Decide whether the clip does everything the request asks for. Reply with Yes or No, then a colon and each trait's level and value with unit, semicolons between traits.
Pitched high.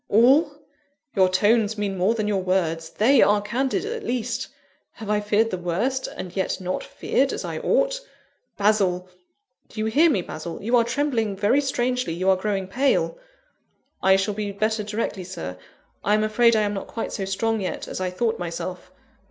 Yes: high, 210 Hz